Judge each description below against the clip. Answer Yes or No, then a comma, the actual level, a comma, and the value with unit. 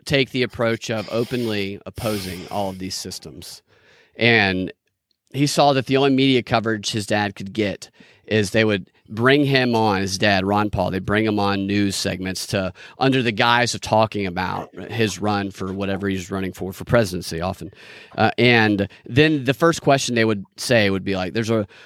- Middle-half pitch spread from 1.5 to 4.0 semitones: Yes, average, 3.6 semitones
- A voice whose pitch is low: Yes, low, 105 Hz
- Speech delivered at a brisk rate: No, average, 190 wpm